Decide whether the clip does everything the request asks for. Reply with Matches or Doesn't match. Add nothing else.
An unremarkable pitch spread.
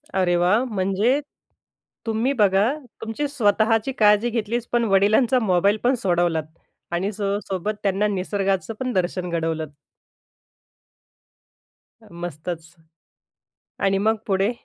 Matches